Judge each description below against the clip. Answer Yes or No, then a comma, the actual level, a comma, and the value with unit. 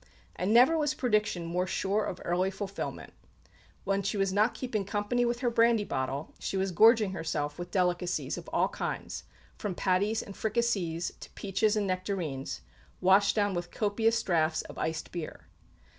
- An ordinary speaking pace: Yes, average, 165 wpm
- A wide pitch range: No, average, 3.5 semitones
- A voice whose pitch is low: No, high, 195 Hz